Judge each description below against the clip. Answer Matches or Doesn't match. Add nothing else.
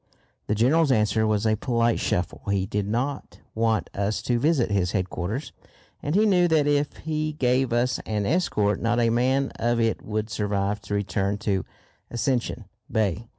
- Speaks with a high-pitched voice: Doesn't match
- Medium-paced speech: Matches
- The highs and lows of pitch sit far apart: Doesn't match